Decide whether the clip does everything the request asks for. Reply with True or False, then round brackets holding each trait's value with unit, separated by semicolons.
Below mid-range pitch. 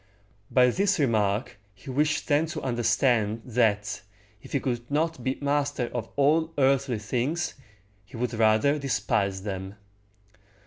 True (125 Hz)